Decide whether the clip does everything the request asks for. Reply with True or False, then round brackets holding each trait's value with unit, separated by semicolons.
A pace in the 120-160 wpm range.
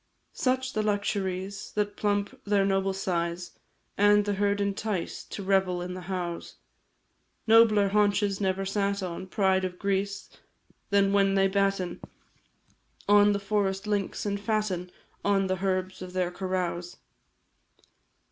True (135 wpm)